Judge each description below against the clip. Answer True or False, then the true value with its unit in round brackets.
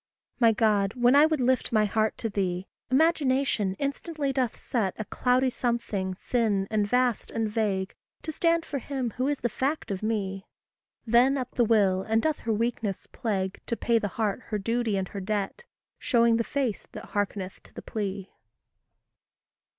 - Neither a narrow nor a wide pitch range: True (4.1 semitones)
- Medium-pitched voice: False (225 Hz)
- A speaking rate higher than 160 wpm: True (175 wpm)